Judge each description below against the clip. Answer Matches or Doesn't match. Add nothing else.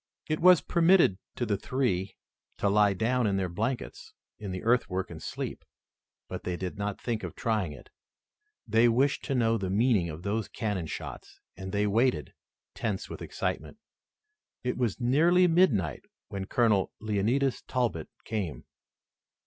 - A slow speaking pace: Doesn't match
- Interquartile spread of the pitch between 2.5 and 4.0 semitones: Doesn't match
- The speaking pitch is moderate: Doesn't match